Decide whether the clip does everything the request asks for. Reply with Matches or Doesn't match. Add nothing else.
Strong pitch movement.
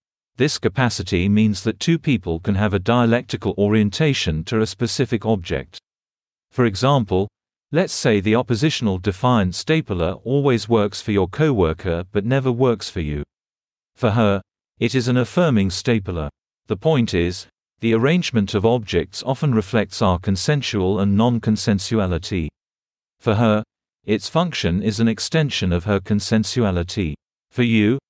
Doesn't match